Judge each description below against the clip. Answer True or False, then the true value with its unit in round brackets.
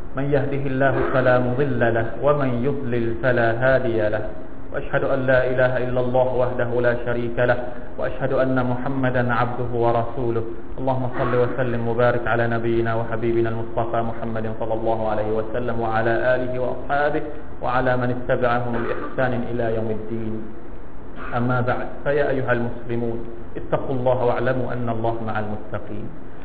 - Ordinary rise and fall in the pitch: False (1.8 semitones)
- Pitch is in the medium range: False (120 Hz)